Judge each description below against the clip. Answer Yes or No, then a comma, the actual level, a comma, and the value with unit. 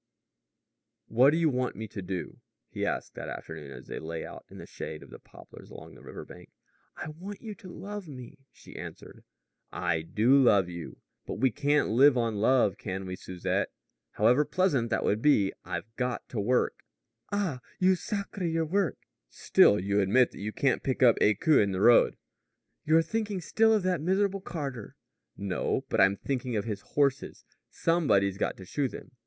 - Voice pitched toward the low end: Yes, low, 125 Hz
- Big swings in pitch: Yes, wide, 8.4 semitones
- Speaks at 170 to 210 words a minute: Yes, average, 185 wpm